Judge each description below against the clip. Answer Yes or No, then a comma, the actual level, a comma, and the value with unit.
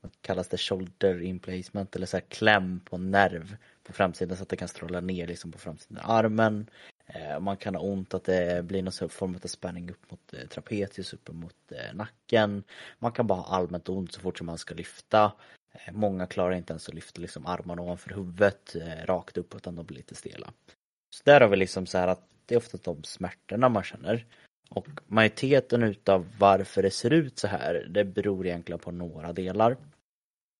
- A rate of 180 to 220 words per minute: Yes, fast, 195 wpm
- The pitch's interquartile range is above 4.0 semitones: No, average, 2.7 semitones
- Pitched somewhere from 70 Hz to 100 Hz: Yes, very low, 95 Hz